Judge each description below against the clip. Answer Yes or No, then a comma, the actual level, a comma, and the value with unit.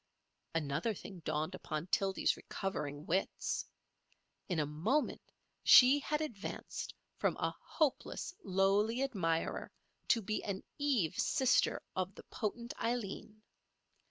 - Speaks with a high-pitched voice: Yes, high, 195 Hz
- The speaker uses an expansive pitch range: Yes, wide, 6.2 semitones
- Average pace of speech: No, slow, 115 wpm